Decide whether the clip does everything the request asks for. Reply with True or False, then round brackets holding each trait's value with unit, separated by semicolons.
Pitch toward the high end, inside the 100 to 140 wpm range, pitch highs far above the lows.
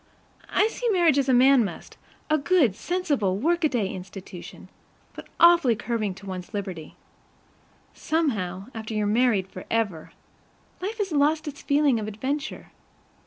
True (245 Hz; 135 wpm; 7.5 semitones)